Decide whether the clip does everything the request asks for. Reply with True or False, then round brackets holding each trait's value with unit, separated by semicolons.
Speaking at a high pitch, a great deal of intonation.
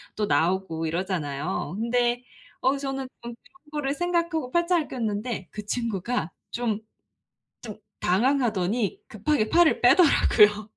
True (235 Hz; 5.8 semitones)